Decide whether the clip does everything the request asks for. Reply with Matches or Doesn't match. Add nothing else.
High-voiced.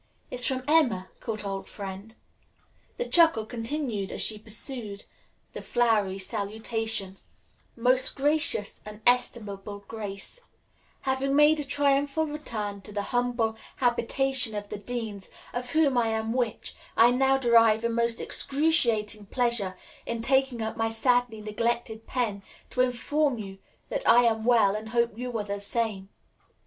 Matches